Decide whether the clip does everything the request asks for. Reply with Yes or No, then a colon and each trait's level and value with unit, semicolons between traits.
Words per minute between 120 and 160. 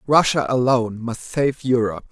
Yes: average, 140 wpm